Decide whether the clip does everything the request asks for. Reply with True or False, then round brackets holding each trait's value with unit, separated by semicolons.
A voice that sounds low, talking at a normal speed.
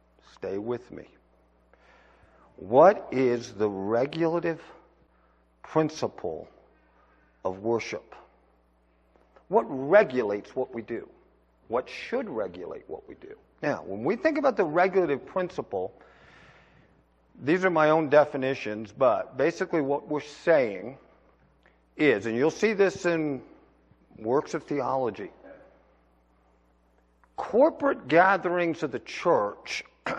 False (130 Hz; 105 wpm)